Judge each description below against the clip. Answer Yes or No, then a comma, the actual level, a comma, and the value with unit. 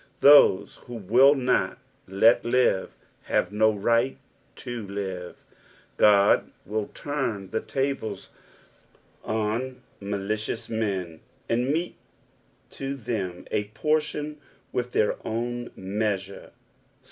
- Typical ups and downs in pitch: Yes, average, 4.1 semitones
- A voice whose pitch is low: Yes, low, 110 Hz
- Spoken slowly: Yes, slow, 100 wpm